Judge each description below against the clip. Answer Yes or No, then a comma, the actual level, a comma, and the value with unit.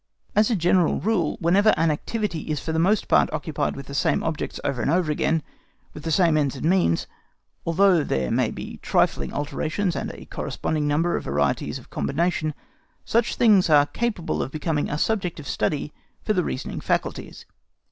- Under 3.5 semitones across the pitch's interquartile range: No, average, 4.0 semitones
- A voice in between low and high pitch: Yes, medium, 160 Hz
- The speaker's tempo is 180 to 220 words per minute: Yes, average, 185 wpm